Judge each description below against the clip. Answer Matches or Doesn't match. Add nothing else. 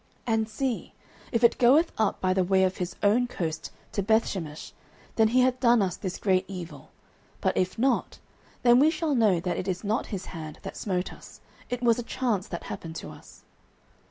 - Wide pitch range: Doesn't match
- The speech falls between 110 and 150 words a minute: Doesn't match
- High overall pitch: Matches